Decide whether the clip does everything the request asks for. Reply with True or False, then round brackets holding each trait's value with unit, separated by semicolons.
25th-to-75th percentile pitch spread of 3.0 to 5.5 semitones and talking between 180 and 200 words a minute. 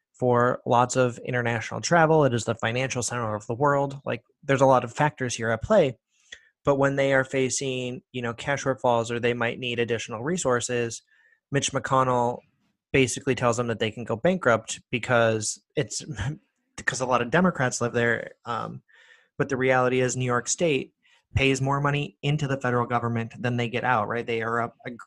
False (2.5 semitones; 190 wpm)